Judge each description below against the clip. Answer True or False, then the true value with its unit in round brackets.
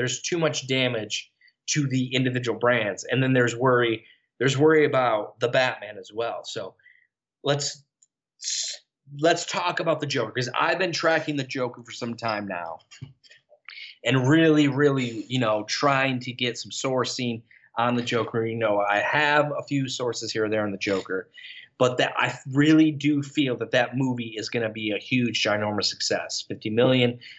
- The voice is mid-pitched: False (130 Hz)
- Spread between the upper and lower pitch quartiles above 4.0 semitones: False (3.7 semitones)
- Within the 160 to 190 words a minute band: True (175 wpm)